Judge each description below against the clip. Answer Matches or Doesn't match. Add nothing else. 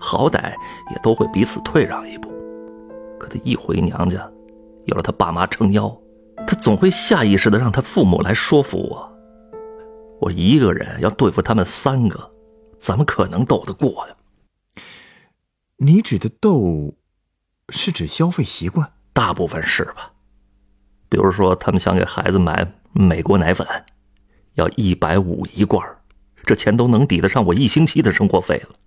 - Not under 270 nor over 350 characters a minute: Doesn't match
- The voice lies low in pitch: Matches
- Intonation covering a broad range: Matches